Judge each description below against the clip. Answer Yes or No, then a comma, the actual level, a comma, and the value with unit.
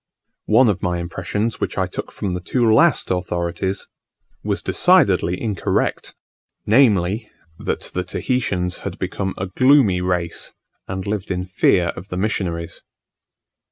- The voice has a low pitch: Yes, very low, 95 Hz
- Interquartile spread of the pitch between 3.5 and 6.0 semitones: No, average, 3.1 semitones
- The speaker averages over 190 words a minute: No, slow, 135 wpm